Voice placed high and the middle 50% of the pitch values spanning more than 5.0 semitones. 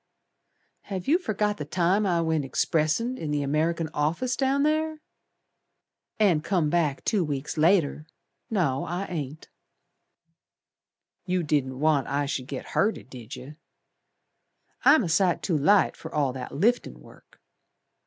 No: medium, 165 Hz; wide, 5.5 semitones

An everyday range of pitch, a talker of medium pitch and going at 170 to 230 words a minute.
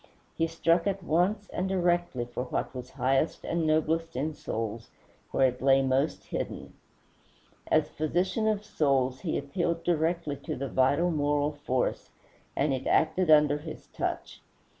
No: average, 4.1 semitones; medium, 155 Hz; average, 150 wpm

